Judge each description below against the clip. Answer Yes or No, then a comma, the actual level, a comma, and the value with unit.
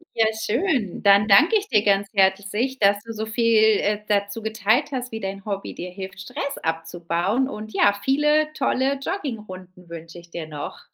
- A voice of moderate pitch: No, high, 210 Hz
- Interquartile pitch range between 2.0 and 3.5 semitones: No, average, 4.4 semitones